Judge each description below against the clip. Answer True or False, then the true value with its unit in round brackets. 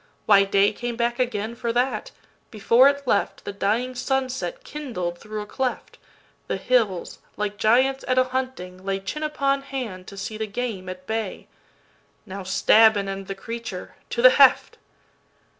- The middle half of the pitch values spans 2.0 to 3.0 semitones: False (4.5 semitones)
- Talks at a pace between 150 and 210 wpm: False (140 wpm)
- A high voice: True (225 Hz)